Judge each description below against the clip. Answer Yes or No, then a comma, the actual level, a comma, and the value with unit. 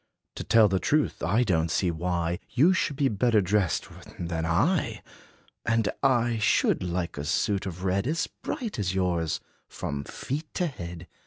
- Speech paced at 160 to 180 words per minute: Yes, average, 170 wpm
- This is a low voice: Yes, very low, 95 Hz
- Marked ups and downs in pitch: Yes, wide, 6.2 semitones